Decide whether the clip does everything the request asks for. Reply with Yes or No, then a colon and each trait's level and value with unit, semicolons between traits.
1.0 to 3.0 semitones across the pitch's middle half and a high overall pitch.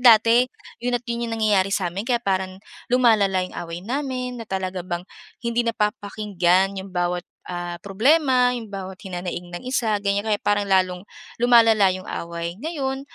No: average, 4.3 semitones; high, 205 Hz